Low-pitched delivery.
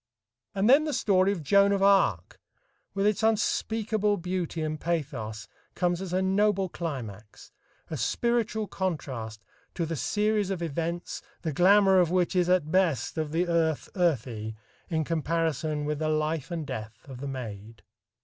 No: medium, 170 Hz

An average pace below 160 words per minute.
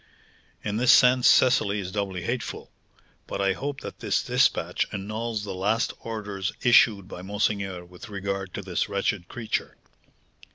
Yes: average, 150 wpm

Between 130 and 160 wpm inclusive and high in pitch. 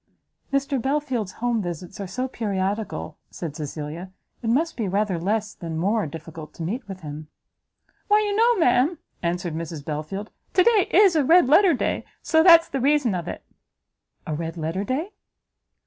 No: average, 175 wpm; high, 210 Hz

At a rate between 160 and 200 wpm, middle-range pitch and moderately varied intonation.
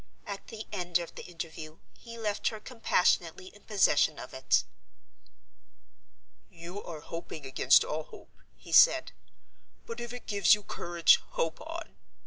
No: average, 145 wpm; medium, 180 Hz; average, 4.5 semitones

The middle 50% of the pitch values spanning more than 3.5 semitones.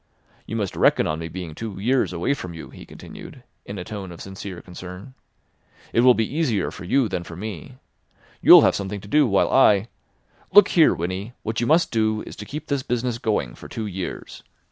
Yes: average, 4.7 semitones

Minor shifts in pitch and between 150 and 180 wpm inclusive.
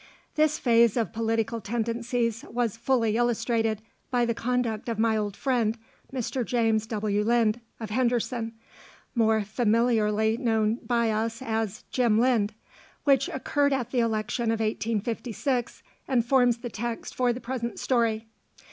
No: narrow, 1.7 semitones; average, 140 wpm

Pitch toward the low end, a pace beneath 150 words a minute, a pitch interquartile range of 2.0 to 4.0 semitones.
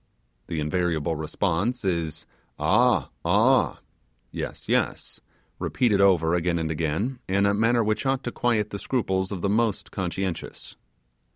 No: very low, 95 Hz; slow, 135 wpm; average, 4.8 semitones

